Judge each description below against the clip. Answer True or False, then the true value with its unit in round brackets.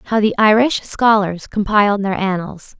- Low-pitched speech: False (205 Hz)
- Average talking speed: True (150 wpm)